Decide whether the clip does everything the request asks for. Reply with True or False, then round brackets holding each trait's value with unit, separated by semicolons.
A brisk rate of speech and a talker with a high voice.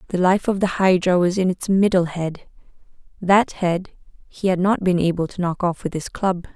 False (210 wpm; 180 Hz)